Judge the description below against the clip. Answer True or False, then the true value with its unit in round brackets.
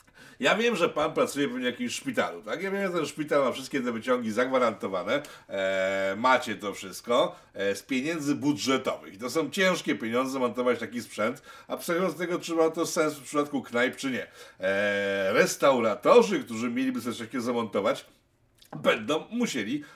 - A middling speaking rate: False (170 wpm)